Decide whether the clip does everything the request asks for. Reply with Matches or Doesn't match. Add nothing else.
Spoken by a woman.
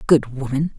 Matches